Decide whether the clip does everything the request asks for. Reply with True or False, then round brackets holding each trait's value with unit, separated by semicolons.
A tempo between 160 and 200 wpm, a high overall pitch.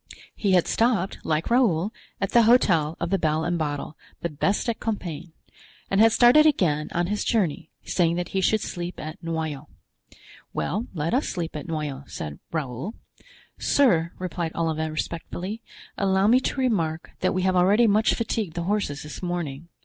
False (170 wpm; 175 Hz)